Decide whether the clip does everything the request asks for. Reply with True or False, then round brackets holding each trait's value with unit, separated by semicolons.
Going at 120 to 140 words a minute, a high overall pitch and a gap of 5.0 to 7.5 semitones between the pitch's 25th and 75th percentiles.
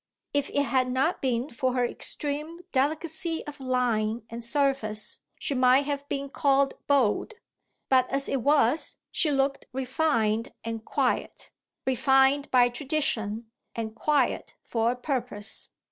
False (135 wpm; 265 Hz; 3.2 semitones)